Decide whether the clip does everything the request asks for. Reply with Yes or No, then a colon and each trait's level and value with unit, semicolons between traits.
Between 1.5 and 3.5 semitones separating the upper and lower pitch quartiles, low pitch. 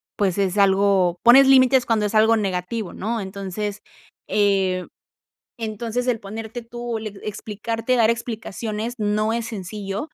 No: narrow, 2.6 semitones; high, 215 Hz